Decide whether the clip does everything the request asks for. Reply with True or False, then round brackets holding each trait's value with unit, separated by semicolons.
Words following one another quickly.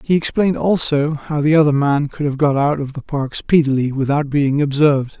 True (210 wpm)